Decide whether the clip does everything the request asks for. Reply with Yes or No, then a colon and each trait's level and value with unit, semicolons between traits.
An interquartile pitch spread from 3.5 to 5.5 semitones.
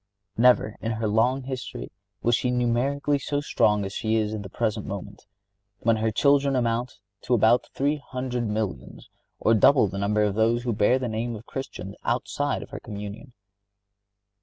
No: average, 3.1 semitones